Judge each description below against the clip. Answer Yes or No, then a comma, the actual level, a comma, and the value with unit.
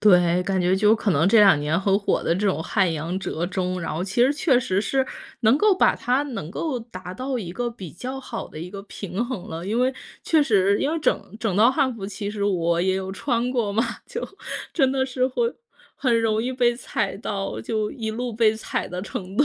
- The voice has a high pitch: Yes, high, 210 Hz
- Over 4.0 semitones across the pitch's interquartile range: Yes, average, 5.0 semitones